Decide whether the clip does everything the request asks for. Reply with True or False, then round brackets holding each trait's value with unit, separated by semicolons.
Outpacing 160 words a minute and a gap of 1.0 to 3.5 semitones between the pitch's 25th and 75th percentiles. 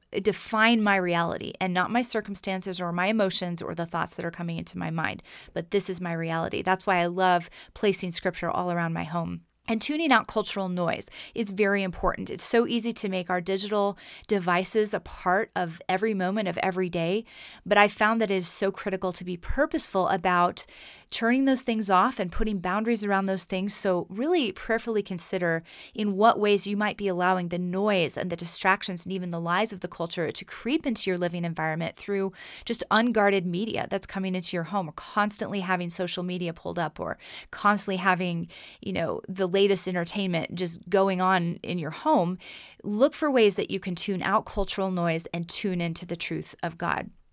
True (200 wpm; 2.9 semitones)